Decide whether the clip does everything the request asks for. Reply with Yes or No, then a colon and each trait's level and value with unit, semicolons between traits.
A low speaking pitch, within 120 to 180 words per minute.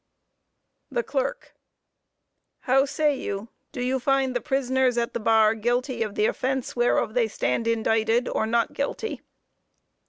No: high, 245 Hz; average, 145 wpm